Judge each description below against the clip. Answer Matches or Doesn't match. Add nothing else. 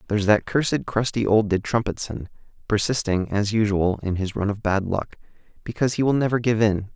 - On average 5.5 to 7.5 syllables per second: Matches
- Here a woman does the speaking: Doesn't match